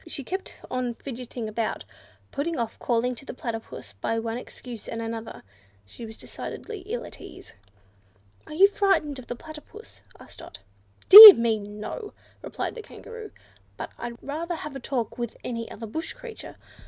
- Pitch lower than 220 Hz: No, very high, 250 Hz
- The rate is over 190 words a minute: No, average, 165 wpm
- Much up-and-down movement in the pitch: Yes, wide, 6.5 semitones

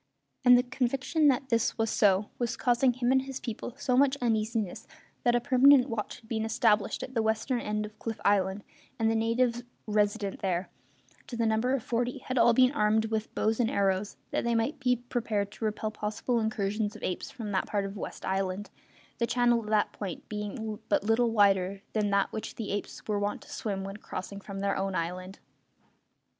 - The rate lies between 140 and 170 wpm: No, average, 200 wpm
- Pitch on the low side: No, high, 220 Hz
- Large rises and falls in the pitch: No, average, 3.0 semitones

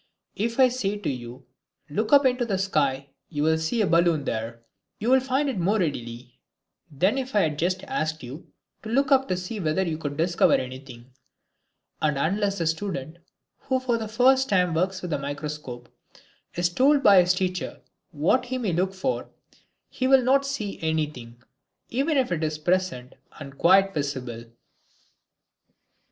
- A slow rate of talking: No, average, 170 wpm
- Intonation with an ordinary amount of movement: No, wide, 7.6 semitones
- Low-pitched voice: No, medium, 180 Hz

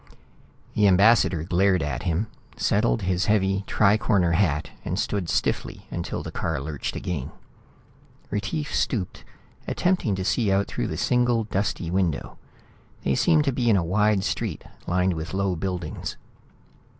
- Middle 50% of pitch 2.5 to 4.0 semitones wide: Yes, average, 3.5 semitones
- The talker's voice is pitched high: No, very low, 95 Hz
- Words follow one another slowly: No, average, 150 wpm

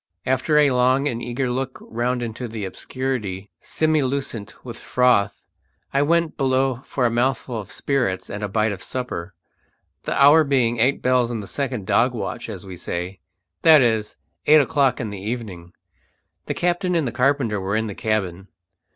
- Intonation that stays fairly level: No, average, 4.1 semitones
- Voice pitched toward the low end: Yes, low, 120 Hz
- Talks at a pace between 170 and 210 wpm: Yes, average, 175 wpm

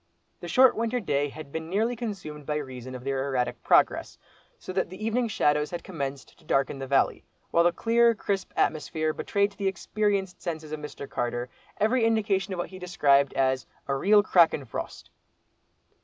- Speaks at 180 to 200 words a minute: Yes, average, 185 wpm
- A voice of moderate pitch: Yes, medium, 170 Hz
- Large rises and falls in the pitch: Yes, wide, 6.6 semitones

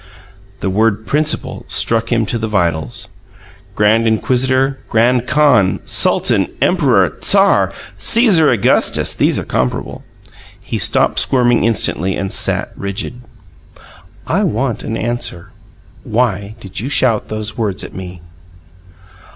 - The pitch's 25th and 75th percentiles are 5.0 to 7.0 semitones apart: No, average, 4.1 semitones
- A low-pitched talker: Yes, low, 115 Hz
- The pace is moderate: No, slow, 120 wpm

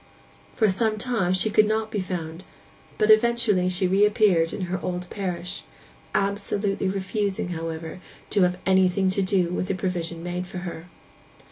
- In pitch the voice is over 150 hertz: Yes, medium, 185 Hz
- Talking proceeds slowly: No, average, 150 wpm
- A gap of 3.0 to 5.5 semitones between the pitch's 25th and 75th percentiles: No, narrow, 2.5 semitones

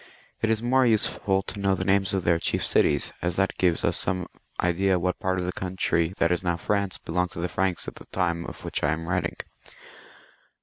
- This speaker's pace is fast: Yes, fast, 230 wpm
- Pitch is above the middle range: No, very low, 90 Hz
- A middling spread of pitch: No, narrow, 1.9 semitones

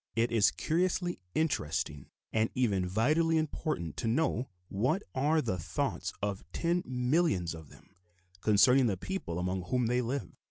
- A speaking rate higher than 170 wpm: No, average, 150 wpm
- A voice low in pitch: Yes, low, 120 Hz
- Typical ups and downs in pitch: No, wide, 8.5 semitones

